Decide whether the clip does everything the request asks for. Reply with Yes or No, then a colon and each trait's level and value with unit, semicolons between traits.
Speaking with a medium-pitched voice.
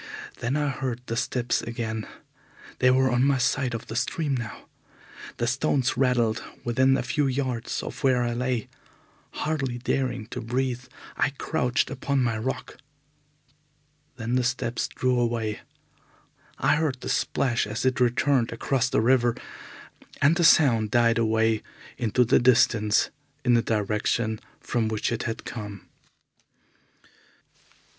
No: low, 120 Hz